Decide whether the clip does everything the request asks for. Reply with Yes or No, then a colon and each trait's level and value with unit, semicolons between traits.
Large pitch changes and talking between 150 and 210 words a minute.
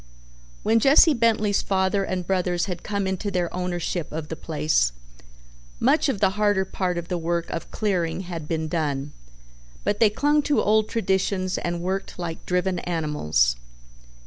No: average, 3.4 semitones; average, 160 wpm